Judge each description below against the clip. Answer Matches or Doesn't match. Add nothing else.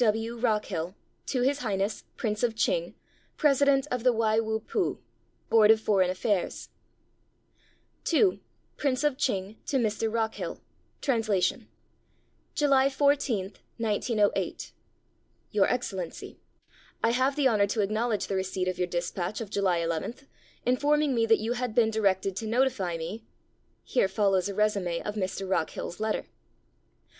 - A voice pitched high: Matches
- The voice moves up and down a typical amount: Matches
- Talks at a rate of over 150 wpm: Doesn't match